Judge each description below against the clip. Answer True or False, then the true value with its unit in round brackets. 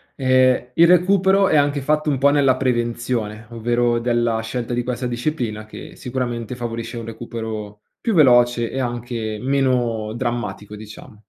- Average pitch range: False (2.3 semitones)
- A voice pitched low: True (120 Hz)